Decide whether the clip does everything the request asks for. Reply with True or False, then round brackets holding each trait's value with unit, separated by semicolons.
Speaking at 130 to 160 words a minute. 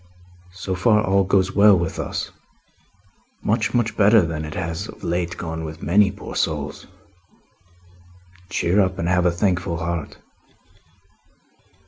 True (135 wpm)